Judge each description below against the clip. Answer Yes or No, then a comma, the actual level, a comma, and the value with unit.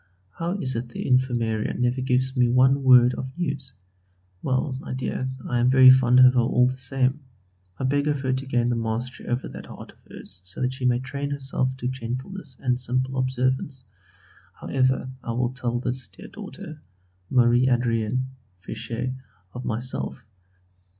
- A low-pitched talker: Yes, low, 130 Hz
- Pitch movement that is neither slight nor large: No, narrow, 1.3 semitones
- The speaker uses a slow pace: No, average, 175 wpm